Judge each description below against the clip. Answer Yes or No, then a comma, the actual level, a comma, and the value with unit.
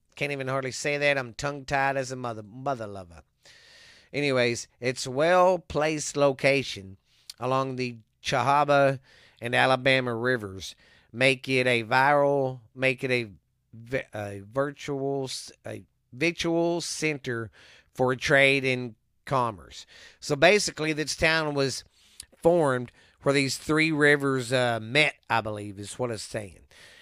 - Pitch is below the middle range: Yes, low, 130 Hz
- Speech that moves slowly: Yes, slow, 125 wpm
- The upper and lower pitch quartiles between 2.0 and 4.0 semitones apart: Yes, average, 3.3 semitones